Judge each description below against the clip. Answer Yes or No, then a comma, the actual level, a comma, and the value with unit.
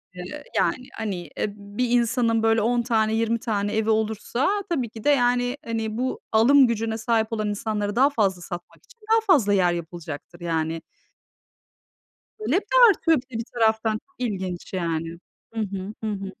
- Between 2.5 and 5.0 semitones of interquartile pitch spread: Yes, average, 3.6 semitones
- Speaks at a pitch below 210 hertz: No, high, 220 Hz